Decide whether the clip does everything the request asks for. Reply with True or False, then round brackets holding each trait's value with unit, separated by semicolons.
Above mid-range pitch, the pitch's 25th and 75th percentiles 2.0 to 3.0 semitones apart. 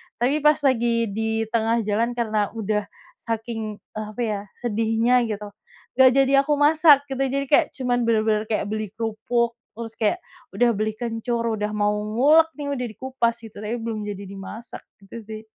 True (225 Hz; 2.4 semitones)